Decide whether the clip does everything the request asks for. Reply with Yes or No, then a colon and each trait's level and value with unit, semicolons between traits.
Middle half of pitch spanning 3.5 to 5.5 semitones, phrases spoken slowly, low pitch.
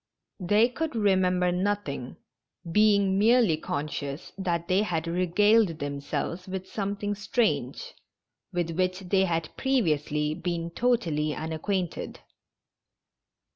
No: average, 3.9 semitones; slow, 105 wpm; medium, 185 Hz